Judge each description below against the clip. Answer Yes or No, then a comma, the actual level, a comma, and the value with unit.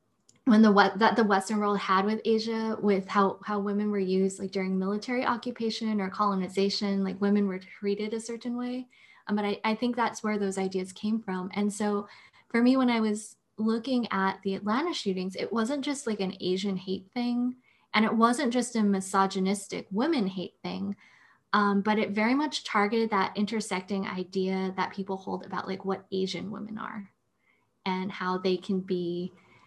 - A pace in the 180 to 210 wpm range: Yes, average, 185 wpm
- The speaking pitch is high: Yes, high, 205 Hz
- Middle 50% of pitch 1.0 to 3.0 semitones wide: Yes, narrow, 2.6 semitones